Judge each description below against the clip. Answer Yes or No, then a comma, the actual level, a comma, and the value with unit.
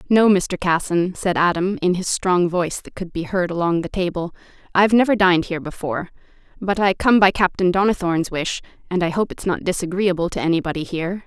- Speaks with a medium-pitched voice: Yes, medium, 180 Hz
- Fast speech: No, average, 195 wpm